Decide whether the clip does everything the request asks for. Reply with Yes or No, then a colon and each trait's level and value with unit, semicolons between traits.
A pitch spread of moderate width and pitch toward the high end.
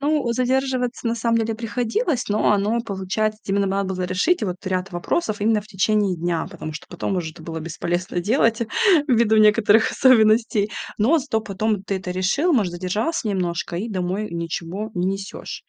Yes: average, 3.8 semitones; high, 210 Hz